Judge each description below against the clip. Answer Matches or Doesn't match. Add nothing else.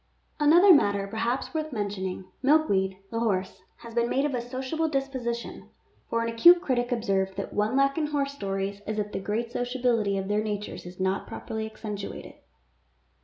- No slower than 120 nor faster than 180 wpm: Matches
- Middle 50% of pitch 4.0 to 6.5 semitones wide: Matches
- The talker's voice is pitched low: Doesn't match